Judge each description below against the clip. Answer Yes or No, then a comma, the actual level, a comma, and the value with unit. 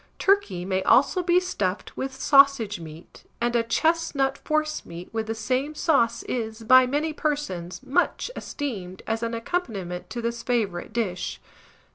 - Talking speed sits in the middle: Yes, average, 145 wpm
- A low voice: No, high, 235 Hz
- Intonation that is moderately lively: No, wide, 5.9 semitones